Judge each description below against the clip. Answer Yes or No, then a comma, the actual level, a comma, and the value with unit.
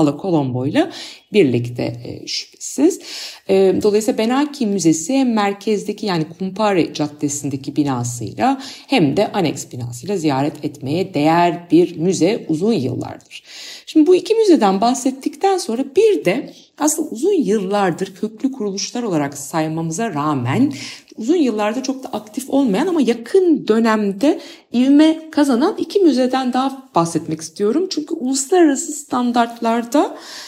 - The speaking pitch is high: Yes, high, 225 Hz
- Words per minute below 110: No, average, 115 wpm